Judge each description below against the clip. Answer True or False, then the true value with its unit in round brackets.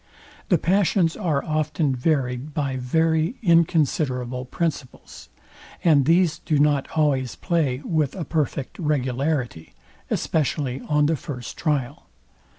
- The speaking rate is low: True (115 wpm)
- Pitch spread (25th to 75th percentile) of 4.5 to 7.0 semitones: False (3.7 semitones)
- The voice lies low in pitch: False (150 Hz)